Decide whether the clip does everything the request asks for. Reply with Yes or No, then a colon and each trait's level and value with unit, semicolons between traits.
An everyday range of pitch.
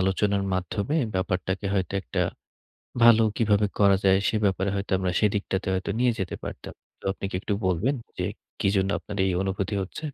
No: narrow, 1.7 semitones